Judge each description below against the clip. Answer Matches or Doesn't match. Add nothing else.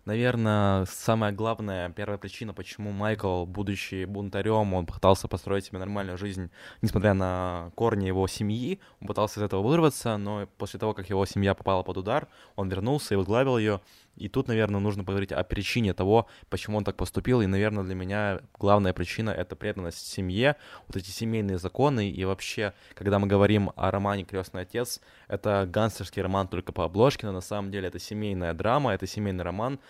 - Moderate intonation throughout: Doesn't match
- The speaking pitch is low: Matches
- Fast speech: Matches